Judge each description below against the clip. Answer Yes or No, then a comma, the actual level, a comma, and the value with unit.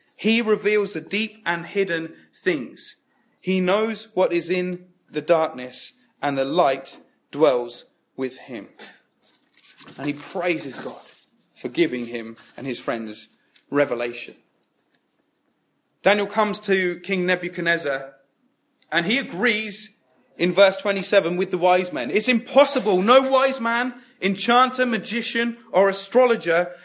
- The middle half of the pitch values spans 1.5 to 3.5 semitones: No, average, 5.1 semitones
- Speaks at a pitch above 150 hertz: Yes, high, 190 Hz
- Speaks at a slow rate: Yes, slow, 125 wpm